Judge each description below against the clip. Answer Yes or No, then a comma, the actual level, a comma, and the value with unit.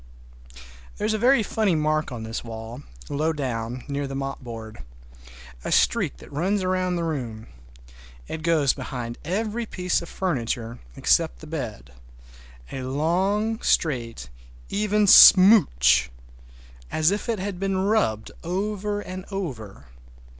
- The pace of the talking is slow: Yes, slow, 130 wpm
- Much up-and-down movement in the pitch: Yes, wide, 8.5 semitones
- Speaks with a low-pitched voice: No, medium, 160 Hz